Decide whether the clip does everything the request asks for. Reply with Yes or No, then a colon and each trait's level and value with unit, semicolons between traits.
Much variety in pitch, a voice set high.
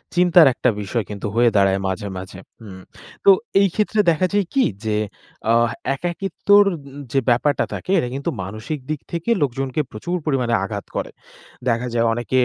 No: wide, 7.9 semitones; low, 130 Hz